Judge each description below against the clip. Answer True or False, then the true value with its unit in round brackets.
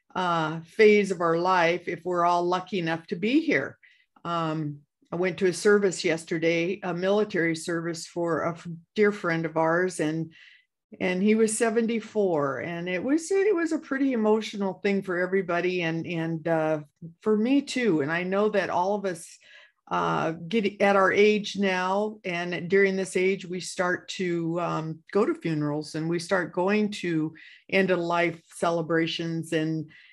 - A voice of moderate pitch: True (180 Hz)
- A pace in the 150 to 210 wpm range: True (170 wpm)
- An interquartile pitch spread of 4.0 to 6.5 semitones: False (3.4 semitones)